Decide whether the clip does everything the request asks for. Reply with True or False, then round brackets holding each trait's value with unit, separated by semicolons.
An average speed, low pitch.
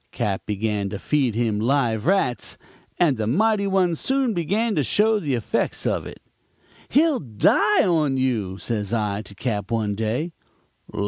True (155 wpm; 125 Hz)